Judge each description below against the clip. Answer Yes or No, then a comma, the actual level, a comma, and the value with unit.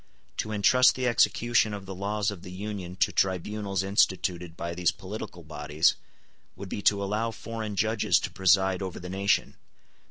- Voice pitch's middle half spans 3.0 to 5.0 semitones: No, narrow, 2.6 semitones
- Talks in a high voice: No, low, 100 Hz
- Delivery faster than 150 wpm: Yes, average, 165 wpm